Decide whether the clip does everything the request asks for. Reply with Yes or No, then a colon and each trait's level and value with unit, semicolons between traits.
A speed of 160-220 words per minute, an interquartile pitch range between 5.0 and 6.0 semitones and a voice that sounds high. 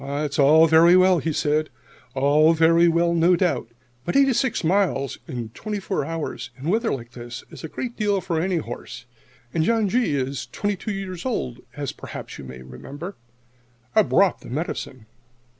No: average, 180 wpm; wide, 5.5 semitones; medium, 165 Hz